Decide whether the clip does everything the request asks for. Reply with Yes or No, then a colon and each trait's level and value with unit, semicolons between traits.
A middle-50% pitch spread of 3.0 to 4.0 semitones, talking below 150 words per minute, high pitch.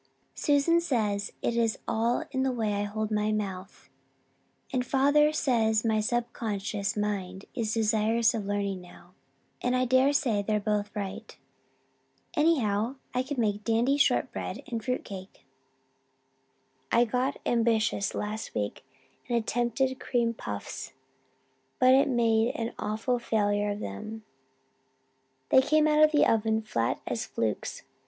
Yes: average, 3.3 semitones; slow, 135 wpm; high, 225 Hz